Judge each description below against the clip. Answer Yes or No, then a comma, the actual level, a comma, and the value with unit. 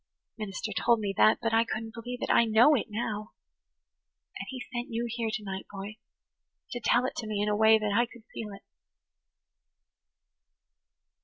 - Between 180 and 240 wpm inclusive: Yes, average, 185 wpm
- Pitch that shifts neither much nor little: No, narrow, 2.0 semitones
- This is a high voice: Yes, high, 220 Hz